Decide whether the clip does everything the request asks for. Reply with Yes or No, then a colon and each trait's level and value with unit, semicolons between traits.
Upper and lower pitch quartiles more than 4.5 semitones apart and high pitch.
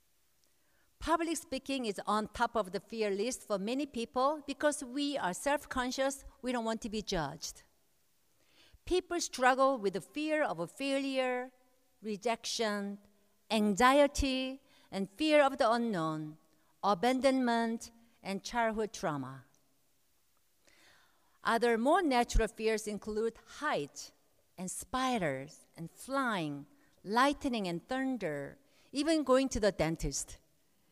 Yes: average, 5.1 semitones; high, 230 Hz